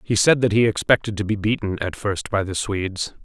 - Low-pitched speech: Yes, low, 105 Hz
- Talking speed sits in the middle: No, fast, 240 wpm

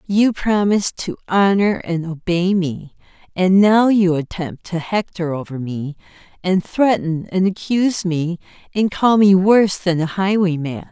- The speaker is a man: No, female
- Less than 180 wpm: Yes, average, 150 wpm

